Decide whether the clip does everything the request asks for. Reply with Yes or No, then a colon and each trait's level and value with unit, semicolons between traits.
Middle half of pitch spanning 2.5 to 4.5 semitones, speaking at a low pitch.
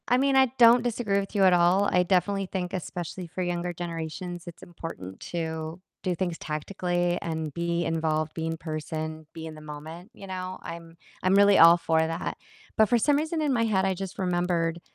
No: average, 2.9 semitones; medium, 175 Hz